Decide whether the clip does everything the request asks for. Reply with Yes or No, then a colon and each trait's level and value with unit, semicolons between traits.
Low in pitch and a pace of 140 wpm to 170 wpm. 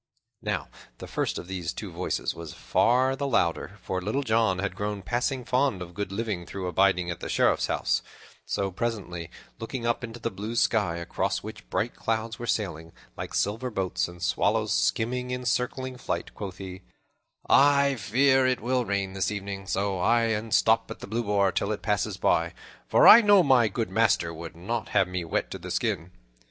No: low, 105 Hz; average, 195 wpm